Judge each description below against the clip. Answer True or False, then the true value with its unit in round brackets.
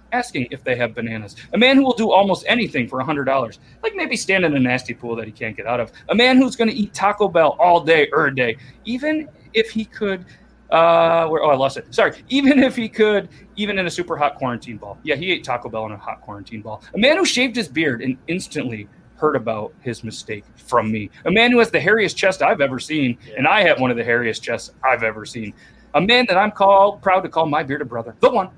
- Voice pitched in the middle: True (165 Hz)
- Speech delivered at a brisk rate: True (255 wpm)